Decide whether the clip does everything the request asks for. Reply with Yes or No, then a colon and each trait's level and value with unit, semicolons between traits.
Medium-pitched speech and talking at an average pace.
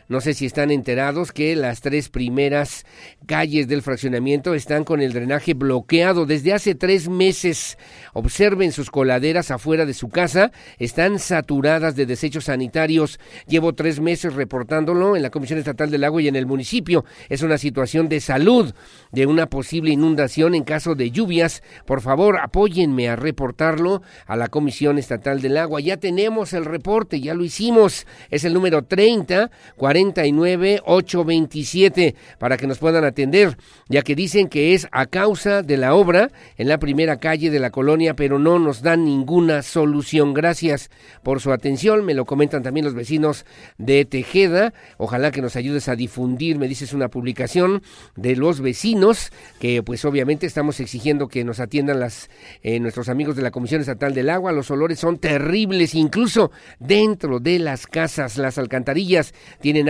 Yes: medium, 150 Hz; average, 165 wpm